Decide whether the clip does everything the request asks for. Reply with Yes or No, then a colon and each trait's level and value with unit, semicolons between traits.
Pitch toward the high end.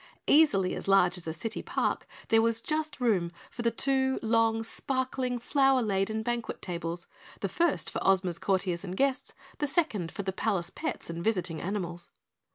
Yes: high, 220 Hz